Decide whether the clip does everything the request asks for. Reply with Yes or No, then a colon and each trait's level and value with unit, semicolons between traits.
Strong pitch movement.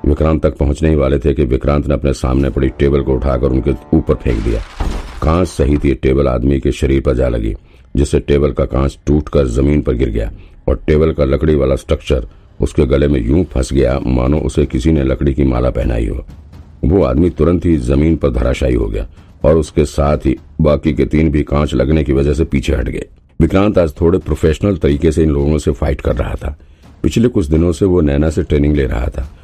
No: narrow, 2.4 semitones